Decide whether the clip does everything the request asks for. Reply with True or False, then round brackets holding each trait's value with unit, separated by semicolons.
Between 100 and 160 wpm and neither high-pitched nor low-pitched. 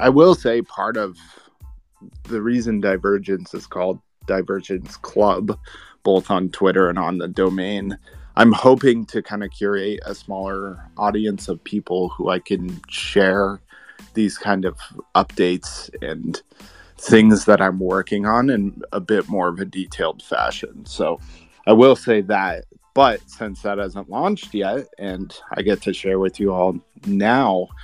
False (155 wpm; 100 Hz)